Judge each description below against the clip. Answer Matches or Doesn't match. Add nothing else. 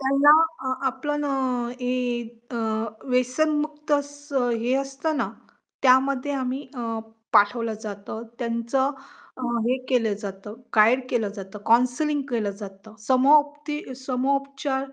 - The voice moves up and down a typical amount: Matches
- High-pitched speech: Matches